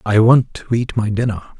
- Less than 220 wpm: No, fast, 225 wpm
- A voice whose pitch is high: No, low, 110 Hz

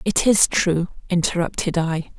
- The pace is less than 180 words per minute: Yes, slow, 135 wpm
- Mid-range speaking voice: Yes, medium, 175 Hz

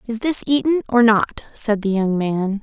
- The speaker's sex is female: Yes, female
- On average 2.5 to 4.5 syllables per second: Yes, 4.4 syllables/s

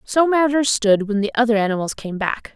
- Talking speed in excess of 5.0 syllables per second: Yes, 5.4 syllables/s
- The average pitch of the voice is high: Yes, high, 230 Hz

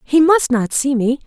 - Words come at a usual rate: No, fast, 235 wpm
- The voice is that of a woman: Yes, female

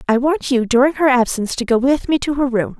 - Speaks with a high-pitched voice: Yes, very high, 260 Hz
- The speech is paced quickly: Yes, fast, 280 wpm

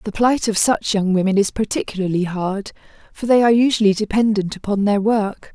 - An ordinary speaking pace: Yes, average, 185 wpm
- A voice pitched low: No, high, 210 Hz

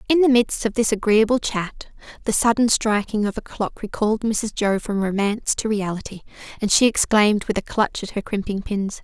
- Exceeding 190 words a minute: Yes, average, 200 wpm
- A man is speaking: No, female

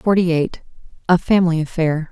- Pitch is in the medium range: Yes, medium, 170 Hz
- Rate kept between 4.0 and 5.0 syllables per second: No, 5.5 syllables/s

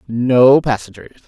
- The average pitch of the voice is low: Yes, low, 120 Hz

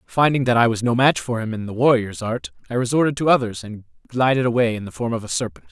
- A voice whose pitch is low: Yes, low, 120 Hz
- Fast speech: Yes, fast, 260 wpm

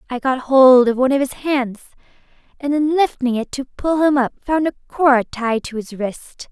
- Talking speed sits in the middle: No, fast, 210 wpm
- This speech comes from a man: No, female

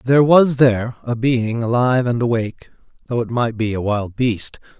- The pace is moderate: Yes, average, 190 wpm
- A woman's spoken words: No, male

